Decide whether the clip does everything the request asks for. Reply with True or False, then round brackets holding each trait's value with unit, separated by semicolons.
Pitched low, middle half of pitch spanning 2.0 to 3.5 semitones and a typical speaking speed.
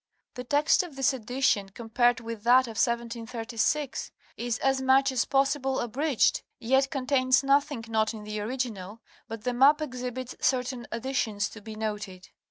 False (245 Hz; 3.1 semitones; 155 wpm)